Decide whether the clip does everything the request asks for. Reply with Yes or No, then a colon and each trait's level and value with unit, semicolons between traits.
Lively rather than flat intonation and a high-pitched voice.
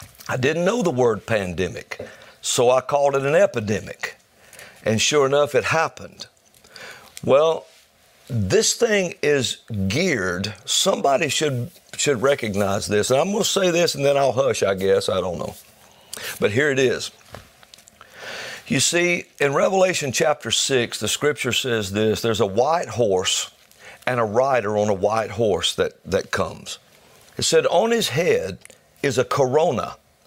No: wide, 8.1 semitones; medium, 140 Hz